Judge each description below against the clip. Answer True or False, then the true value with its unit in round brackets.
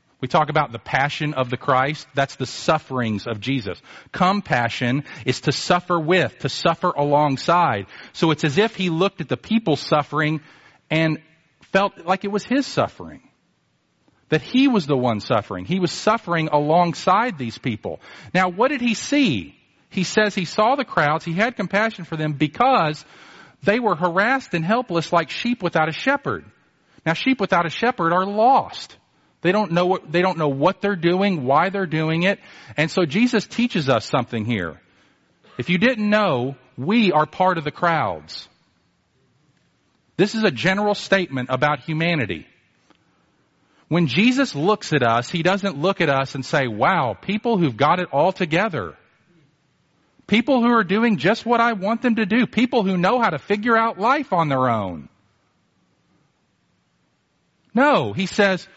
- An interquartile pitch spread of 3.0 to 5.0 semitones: False (5.6 semitones)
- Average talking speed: True (170 wpm)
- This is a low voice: False (170 Hz)